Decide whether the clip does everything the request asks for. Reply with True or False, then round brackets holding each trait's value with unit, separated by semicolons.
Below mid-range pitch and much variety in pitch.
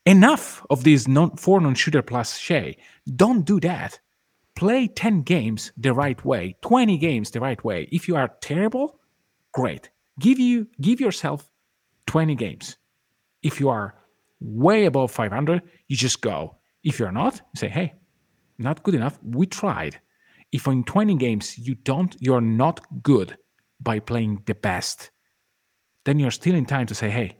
False (145 Hz; 7.0 semitones)